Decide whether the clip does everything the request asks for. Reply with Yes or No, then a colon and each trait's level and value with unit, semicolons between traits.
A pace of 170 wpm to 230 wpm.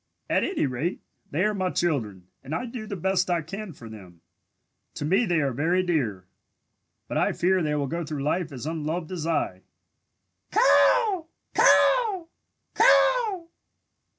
No: average, 155 wpm